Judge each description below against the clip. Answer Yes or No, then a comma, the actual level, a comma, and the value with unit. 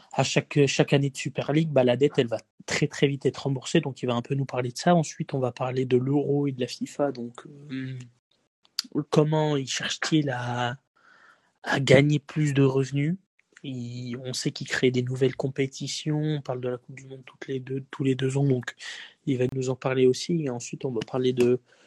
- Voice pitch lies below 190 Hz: Yes, low, 135 Hz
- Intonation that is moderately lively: No, narrow, 2.3 semitones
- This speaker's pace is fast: Yes, fast, 225 wpm